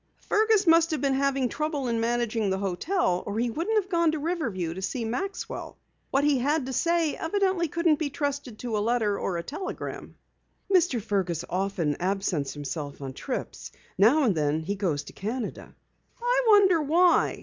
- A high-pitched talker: Yes, very high, 255 Hz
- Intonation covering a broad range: Yes, wide, 9.0 semitones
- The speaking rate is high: No, average, 180 wpm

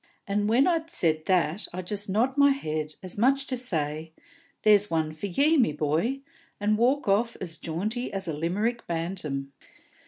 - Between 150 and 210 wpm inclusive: Yes, average, 180 wpm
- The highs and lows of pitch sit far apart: Yes, wide, 7.0 semitones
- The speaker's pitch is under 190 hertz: No, high, 200 Hz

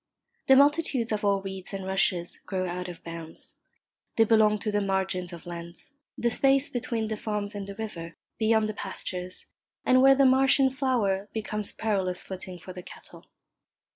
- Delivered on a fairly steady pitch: No, average, 3.8 semitones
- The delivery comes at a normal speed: Yes, average, 175 wpm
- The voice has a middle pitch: No, high, 205 Hz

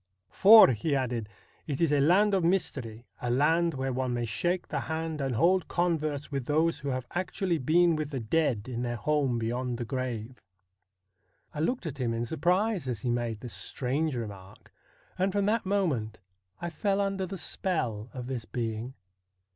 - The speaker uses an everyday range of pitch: No, wide, 6.1 semitones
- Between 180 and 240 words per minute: Yes, average, 185 wpm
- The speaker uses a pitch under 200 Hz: Yes, medium, 140 Hz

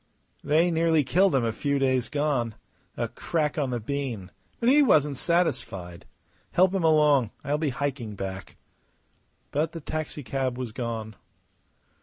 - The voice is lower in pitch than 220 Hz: Yes, medium, 140 Hz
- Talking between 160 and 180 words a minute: No, average, 145 wpm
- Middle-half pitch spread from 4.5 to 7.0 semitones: Yes, average, 4.8 semitones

